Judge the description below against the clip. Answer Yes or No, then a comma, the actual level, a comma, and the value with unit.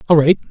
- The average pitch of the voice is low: No, medium, 160 Hz